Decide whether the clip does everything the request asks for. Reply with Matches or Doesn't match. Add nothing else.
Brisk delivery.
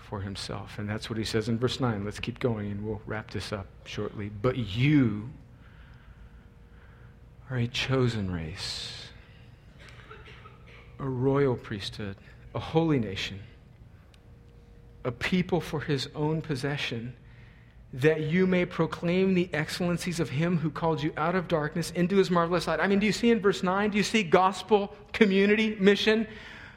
Doesn't match